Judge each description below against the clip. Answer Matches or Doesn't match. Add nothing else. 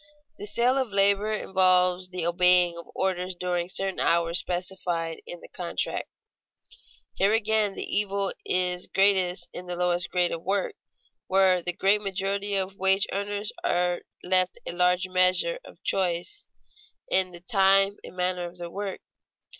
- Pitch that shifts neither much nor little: Doesn't match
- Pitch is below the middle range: Doesn't match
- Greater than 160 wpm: Doesn't match